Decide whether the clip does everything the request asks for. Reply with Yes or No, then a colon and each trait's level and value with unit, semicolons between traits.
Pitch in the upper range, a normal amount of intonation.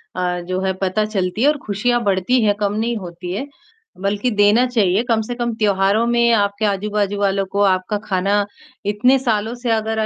Yes: high, 205 Hz; average, 3.0 semitones